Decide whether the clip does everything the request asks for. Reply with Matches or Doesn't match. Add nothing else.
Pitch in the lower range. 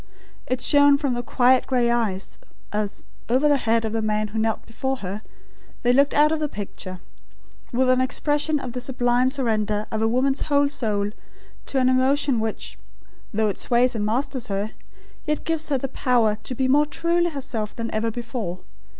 Doesn't match